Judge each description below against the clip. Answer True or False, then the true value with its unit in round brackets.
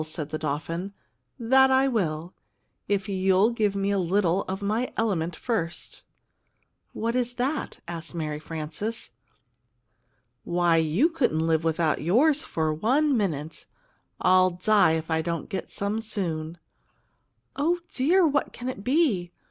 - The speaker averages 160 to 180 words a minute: False (140 wpm)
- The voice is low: False (190 Hz)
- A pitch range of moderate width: False (6.3 semitones)